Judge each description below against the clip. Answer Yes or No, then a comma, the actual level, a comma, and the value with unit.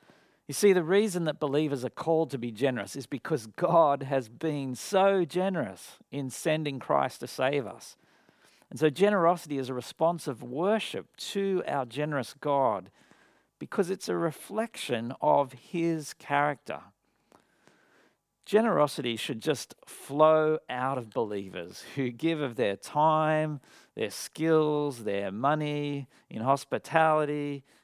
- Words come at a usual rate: No, slow, 130 wpm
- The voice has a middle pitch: Yes, medium, 150 Hz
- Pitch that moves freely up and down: No, average, 3.4 semitones